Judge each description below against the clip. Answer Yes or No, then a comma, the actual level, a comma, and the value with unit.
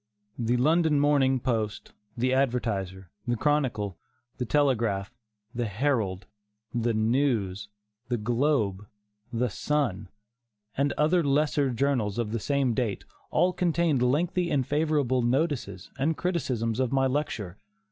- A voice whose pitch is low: Yes, low, 125 Hz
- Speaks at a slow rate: Yes, slow, 125 wpm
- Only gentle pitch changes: No, average, 4.8 semitones